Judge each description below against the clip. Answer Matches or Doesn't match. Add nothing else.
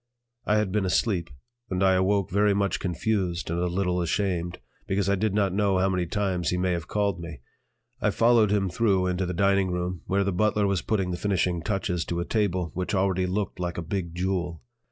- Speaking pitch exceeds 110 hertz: Doesn't match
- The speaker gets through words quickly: Matches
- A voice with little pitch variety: Matches